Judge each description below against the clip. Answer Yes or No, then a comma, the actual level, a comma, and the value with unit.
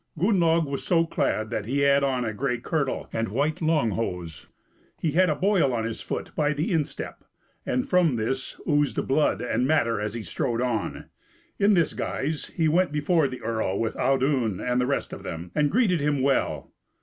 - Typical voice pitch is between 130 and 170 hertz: Yes, medium, 140 Hz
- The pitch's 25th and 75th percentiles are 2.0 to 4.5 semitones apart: No, average, 5.3 semitones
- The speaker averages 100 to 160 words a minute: No, average, 195 wpm